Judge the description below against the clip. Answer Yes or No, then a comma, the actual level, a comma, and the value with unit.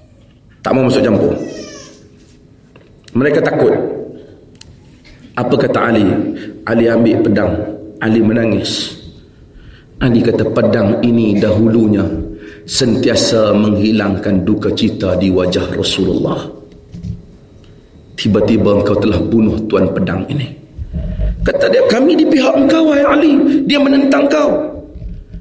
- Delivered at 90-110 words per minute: Yes, average, 105 wpm